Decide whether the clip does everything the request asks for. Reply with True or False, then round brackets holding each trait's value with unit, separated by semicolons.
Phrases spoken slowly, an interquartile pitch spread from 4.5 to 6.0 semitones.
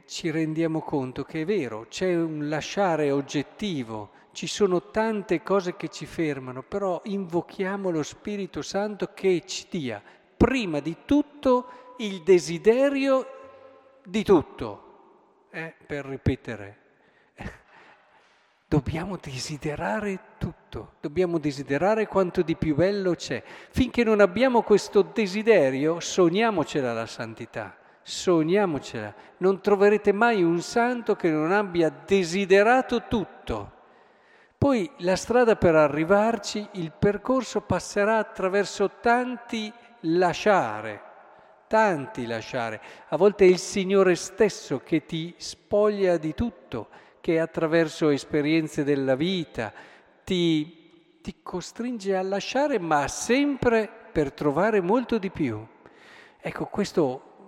True (110 wpm; 5.3 semitones)